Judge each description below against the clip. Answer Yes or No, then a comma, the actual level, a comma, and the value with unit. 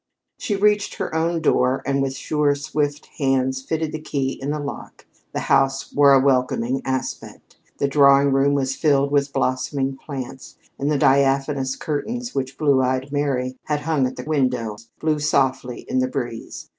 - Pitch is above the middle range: No, medium, 140 Hz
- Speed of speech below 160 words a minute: No, average, 170 wpm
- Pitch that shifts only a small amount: Yes, narrow, 1.9 semitones